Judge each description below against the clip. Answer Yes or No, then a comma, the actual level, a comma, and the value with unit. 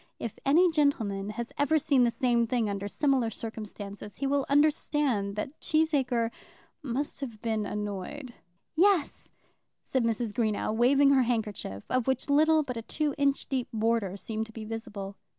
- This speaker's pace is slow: No, average, 160 wpm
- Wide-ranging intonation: No, average, 4.7 semitones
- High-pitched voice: Yes, high, 240 Hz